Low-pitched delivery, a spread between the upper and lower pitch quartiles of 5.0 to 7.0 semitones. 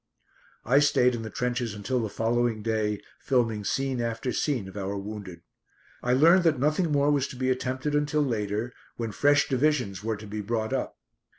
No: low, 120 Hz; average, 4.1 semitones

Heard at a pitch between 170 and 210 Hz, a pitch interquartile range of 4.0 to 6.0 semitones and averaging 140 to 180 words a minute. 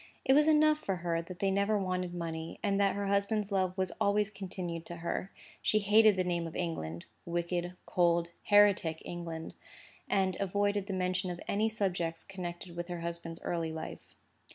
No: medium, 185 Hz; average, 2.8 semitones; average, 170 wpm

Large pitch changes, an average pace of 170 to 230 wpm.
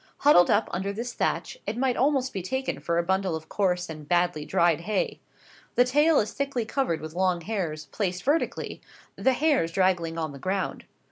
Yes: wide, 6.7 semitones; average, 190 wpm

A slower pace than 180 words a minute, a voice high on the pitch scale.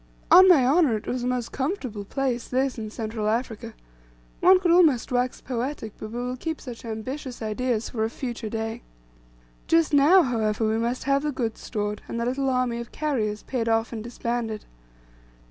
No: average, 185 wpm; high, 245 Hz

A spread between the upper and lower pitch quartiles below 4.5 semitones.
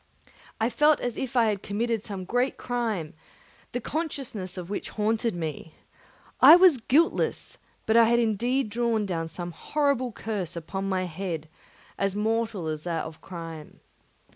No: average, 5.0 semitones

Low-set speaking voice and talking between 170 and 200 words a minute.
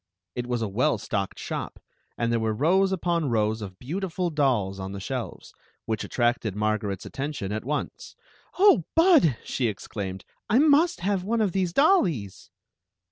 Yes: low, 130 Hz; average, 175 wpm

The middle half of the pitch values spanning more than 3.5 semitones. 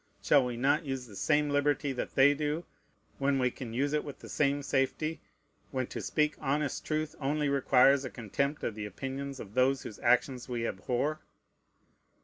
No: narrow, 2.6 semitones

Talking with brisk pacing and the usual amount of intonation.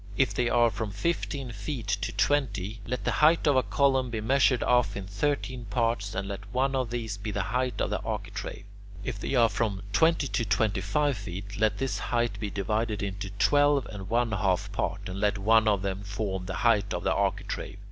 Yes: fast, 210 wpm; average, 4.0 semitones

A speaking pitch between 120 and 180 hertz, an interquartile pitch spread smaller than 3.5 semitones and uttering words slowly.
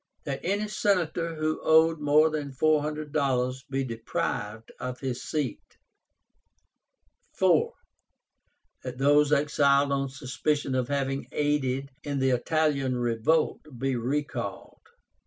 Yes: medium, 140 Hz; average, 2.8 semitones; slow, 120 wpm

